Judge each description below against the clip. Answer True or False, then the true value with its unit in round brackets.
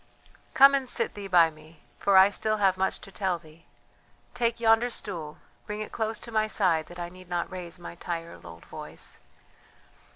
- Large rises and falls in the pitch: False (4.2 semitones)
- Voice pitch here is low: False (185 Hz)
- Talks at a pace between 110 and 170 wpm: False (190 wpm)